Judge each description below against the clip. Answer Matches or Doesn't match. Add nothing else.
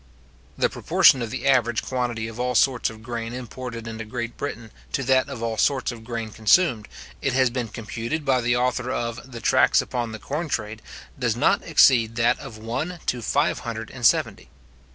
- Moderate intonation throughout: Doesn't match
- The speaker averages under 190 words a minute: Doesn't match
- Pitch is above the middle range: Doesn't match